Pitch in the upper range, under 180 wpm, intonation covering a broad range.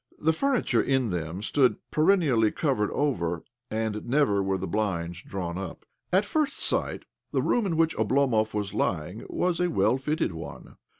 No: low, 110 Hz; average, 165 wpm; wide, 8.1 semitones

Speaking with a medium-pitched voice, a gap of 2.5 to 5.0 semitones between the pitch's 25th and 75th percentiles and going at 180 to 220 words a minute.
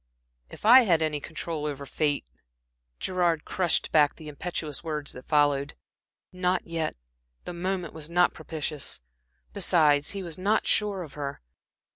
No: medium, 160 Hz; average, 3.3 semitones; average, 145 wpm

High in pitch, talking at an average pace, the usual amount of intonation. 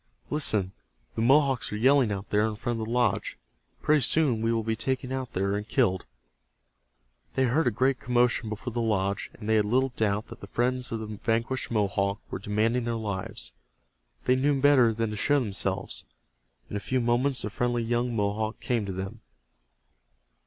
No: low, 115 Hz; average, 190 wpm; average, 3.2 semitones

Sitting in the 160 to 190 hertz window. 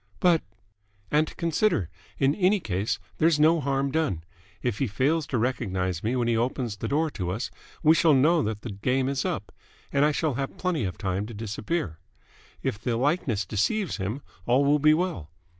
No: low, 130 Hz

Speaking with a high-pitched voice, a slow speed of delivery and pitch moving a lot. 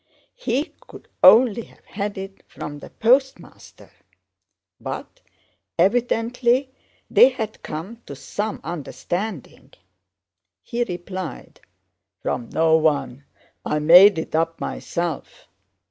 Yes: high, 195 Hz; slow, 100 wpm; wide, 6.5 semitones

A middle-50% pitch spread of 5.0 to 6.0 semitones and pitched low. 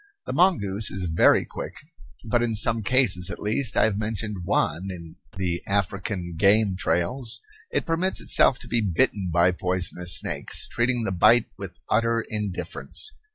No: average, 4.2 semitones; low, 100 Hz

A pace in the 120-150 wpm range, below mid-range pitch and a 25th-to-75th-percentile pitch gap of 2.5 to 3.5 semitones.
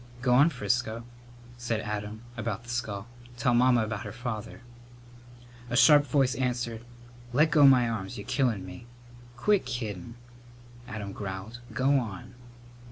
Yes: average, 140 wpm; low, 120 Hz; average, 2.9 semitones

